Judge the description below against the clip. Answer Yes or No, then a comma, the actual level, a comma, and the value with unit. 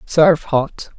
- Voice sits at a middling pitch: Yes, medium, 160 Hz